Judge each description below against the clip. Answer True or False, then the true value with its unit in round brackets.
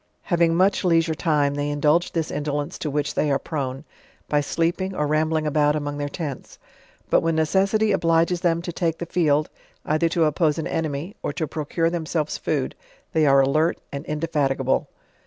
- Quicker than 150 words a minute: True (175 wpm)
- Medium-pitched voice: True (155 Hz)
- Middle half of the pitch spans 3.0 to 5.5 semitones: False (2.4 semitones)